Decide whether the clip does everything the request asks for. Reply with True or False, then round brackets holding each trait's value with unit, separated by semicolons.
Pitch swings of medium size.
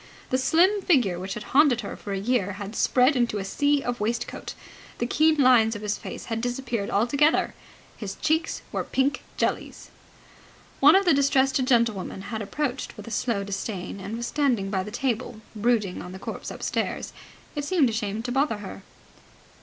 True (4.9 semitones)